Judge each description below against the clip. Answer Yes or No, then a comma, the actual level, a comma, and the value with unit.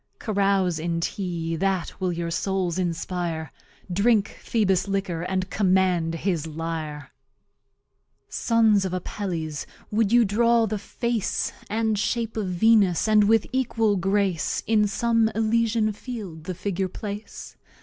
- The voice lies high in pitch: Yes, high, 195 Hz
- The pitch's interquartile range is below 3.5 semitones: No, average, 3.8 semitones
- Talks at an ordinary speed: No, slow, 130 wpm